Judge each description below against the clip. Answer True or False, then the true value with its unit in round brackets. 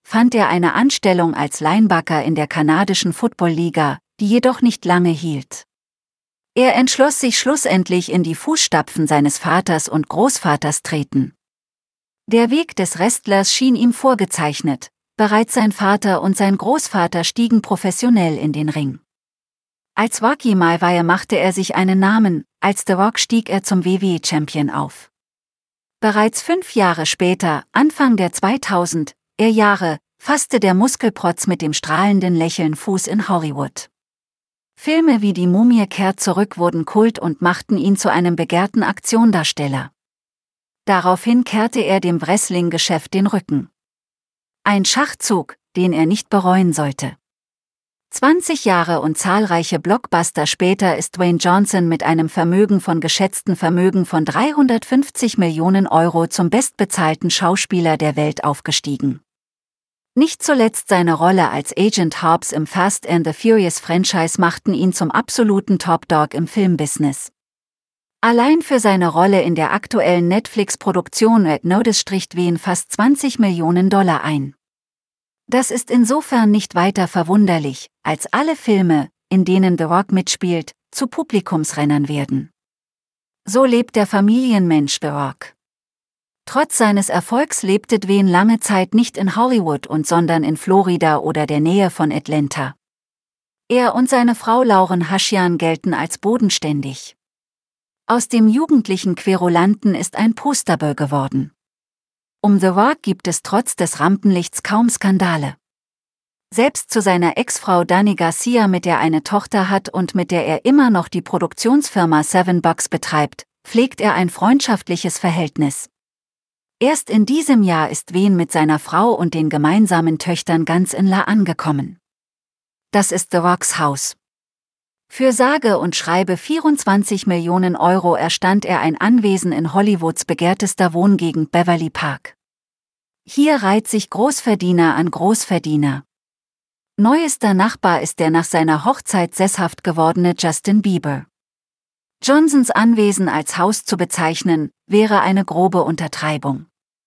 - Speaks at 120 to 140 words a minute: True (135 wpm)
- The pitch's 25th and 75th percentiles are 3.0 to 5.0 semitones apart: True (4.6 semitones)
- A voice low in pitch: False (185 Hz)